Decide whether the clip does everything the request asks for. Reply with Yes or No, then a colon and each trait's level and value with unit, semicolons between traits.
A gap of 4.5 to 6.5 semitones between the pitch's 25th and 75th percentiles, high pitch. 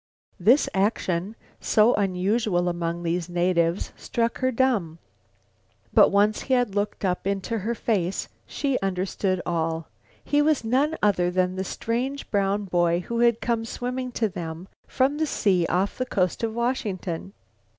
Yes: average, 4.8 semitones; high, 200 Hz